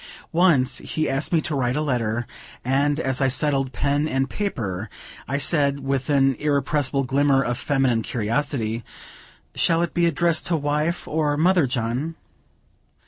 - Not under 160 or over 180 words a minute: No, average, 150 wpm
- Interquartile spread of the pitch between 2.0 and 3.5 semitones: Yes, average, 2.9 semitones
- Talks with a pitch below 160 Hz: Yes, medium, 140 Hz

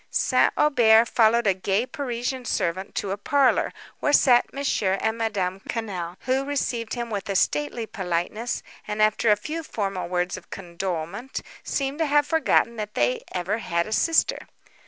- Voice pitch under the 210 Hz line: No, high, 220 Hz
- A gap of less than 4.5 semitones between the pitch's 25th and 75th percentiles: No, average, 5.0 semitones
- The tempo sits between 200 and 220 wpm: No, average, 165 wpm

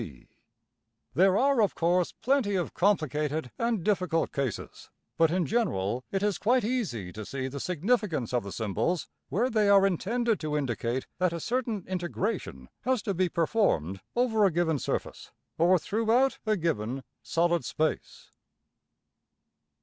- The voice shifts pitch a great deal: Yes, wide, 6.6 semitones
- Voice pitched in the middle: Yes, medium, 180 Hz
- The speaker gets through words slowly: No, average, 150 wpm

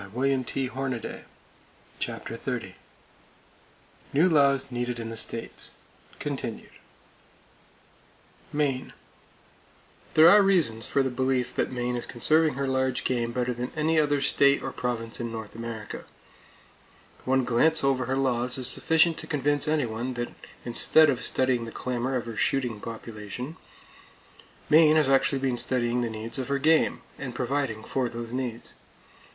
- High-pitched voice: No, low, 130 Hz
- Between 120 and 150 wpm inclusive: Yes, average, 145 wpm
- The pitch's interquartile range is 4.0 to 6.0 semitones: No, average, 2.7 semitones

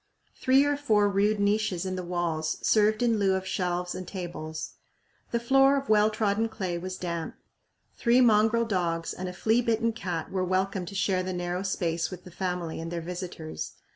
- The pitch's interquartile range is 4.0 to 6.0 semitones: No, average, 3.6 semitones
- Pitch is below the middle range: No, high, 190 Hz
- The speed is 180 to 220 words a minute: Yes, average, 190 wpm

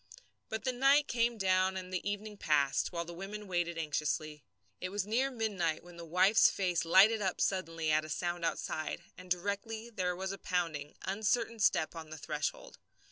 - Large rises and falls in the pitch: No, average, 4.0 semitones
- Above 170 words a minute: Yes, average, 185 wpm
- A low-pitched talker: No, medium, 185 Hz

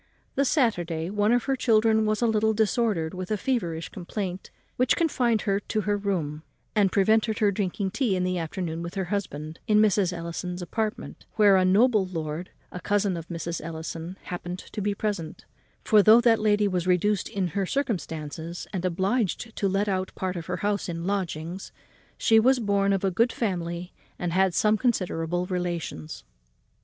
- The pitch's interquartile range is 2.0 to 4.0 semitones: Yes, average, 3.6 semitones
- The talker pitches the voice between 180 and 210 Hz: Yes, high, 190 Hz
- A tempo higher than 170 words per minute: Yes, average, 180 wpm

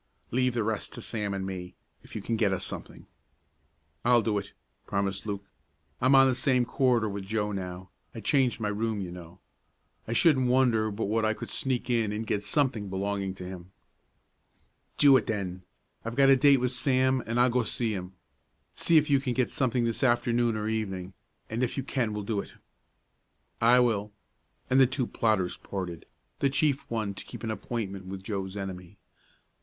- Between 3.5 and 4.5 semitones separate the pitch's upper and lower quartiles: Yes, average, 4.1 semitones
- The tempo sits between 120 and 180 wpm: No, average, 190 wpm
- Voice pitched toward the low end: Yes, low, 110 Hz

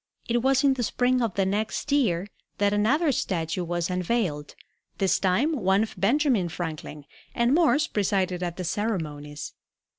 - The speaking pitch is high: Yes, high, 200 Hz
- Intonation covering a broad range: Yes, wide, 5.9 semitones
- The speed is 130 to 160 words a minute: Yes, average, 155 wpm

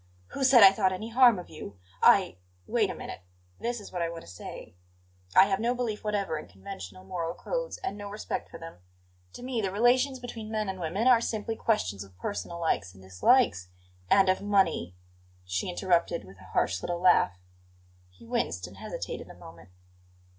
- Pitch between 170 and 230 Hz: Yes, medium, 185 Hz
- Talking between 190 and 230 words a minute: Yes, average, 195 wpm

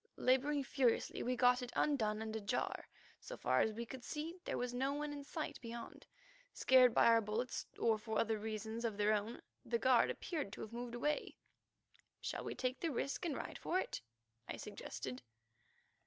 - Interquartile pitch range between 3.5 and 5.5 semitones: Yes, average, 4.0 semitones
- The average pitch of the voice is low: No, high, 245 Hz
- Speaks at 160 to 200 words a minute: Yes, average, 190 wpm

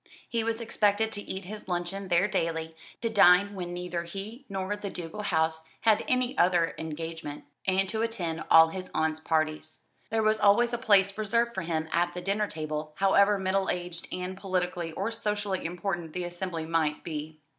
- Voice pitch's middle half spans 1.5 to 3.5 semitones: No, average, 3.9 semitones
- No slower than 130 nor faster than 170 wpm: No, average, 180 wpm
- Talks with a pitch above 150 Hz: Yes, medium, 185 Hz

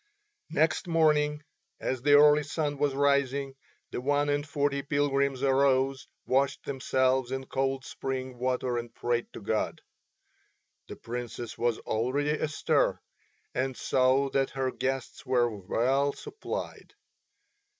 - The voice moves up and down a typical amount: No, narrow, 1.9 semitones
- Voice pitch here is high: No, low, 135 Hz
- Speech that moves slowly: Yes, slow, 125 wpm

